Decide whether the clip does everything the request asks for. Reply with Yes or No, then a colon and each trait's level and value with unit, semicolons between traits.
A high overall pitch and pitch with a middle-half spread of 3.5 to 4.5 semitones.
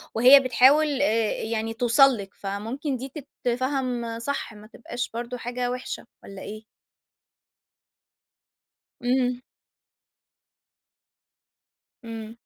No: high, 245 Hz; narrow, 2.4 semitones